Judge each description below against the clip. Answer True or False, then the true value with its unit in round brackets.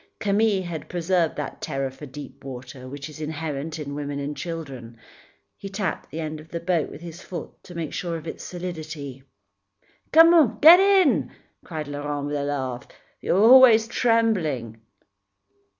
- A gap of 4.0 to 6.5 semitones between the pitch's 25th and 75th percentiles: True (4.7 semitones)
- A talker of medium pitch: True (160 Hz)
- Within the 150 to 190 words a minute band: True (160 wpm)